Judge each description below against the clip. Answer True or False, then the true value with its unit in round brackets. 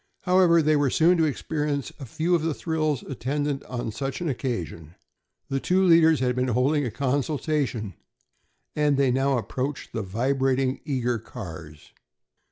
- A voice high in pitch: False (135 Hz)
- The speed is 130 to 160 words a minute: True (155 wpm)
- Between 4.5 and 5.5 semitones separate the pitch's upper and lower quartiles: False (3.7 semitones)